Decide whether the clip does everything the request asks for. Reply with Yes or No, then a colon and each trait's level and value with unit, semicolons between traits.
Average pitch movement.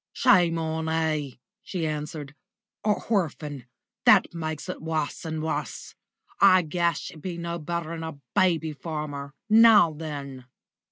No: narrow, 2.2 semitones